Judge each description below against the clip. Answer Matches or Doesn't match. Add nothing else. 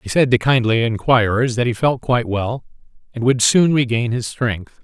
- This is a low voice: Matches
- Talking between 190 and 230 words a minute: Matches